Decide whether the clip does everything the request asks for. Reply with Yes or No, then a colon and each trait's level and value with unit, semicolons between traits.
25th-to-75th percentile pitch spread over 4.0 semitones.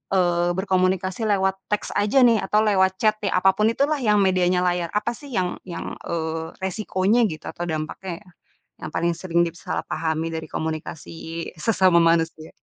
No: average, 2.9 semitones